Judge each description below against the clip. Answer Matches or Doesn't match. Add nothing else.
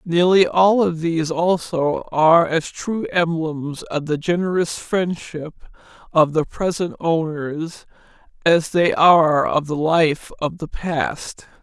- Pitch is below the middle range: Doesn't match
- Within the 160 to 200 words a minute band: Doesn't match